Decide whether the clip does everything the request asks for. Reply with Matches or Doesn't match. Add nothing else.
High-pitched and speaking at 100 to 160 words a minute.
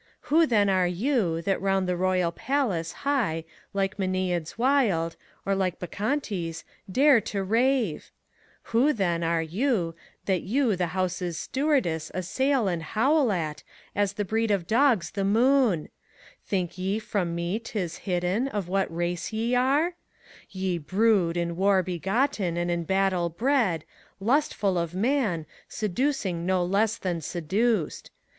Matches